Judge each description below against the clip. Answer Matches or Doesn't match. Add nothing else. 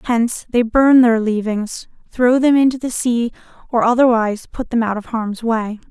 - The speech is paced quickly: Doesn't match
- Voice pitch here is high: Matches